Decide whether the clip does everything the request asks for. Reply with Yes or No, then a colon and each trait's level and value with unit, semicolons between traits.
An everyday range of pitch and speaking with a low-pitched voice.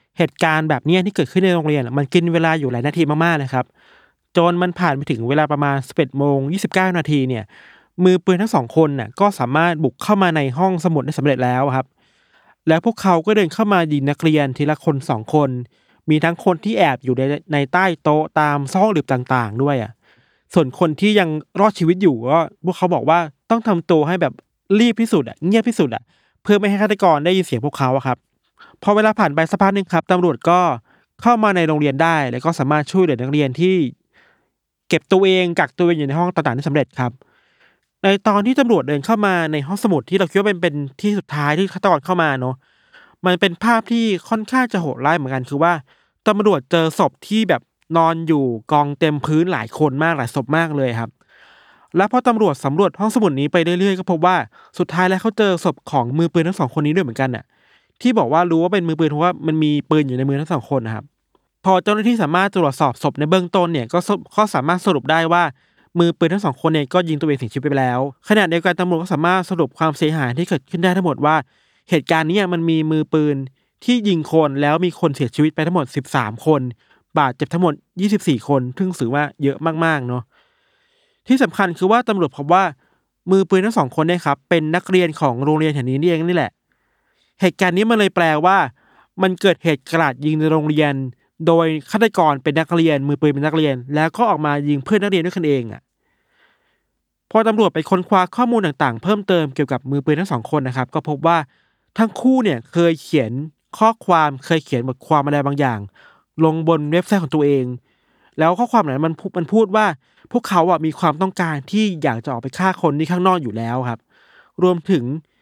No: average, 4.4 semitones; medium, 165 Hz